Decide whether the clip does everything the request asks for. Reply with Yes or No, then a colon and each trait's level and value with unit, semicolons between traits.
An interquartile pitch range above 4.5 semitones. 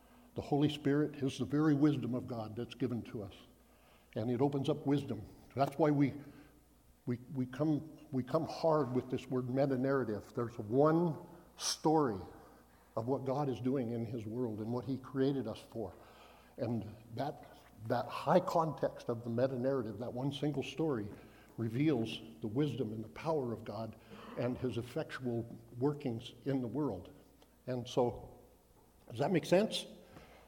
No: average, 3.7 semitones